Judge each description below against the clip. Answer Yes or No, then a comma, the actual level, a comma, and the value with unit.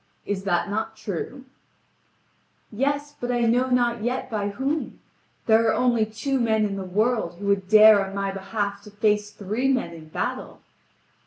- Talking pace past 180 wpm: No, average, 170 wpm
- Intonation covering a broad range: No, average, 3.3 semitones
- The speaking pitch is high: Yes, high, 215 Hz